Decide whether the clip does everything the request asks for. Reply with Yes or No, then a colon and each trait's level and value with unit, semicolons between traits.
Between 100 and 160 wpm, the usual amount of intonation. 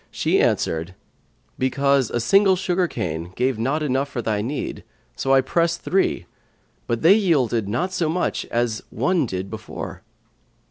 No: average, 150 wpm; wide, 7.0 semitones